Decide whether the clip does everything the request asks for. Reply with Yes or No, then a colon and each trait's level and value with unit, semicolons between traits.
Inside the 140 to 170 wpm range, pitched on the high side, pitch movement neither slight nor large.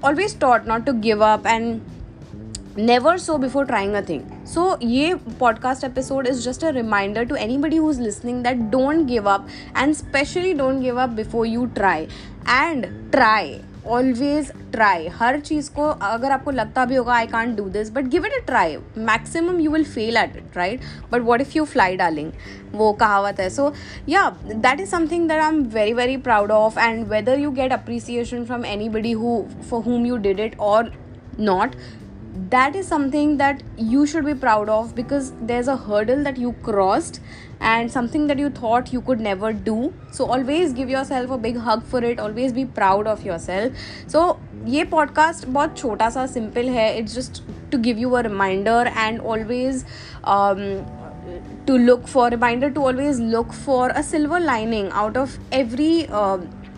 No: average, 185 wpm; high, 245 Hz; average, 4.0 semitones